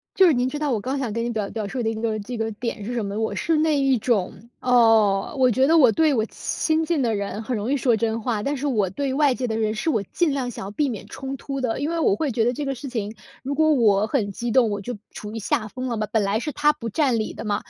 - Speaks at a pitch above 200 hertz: Yes, high, 240 Hz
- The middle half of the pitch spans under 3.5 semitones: No, average, 4.1 semitones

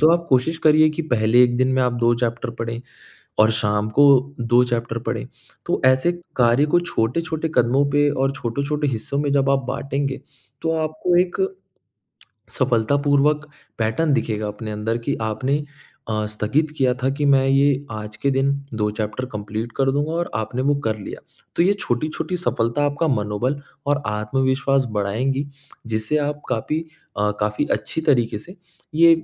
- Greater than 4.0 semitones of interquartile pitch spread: Yes, average, 4.5 semitones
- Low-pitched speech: Yes, low, 130 Hz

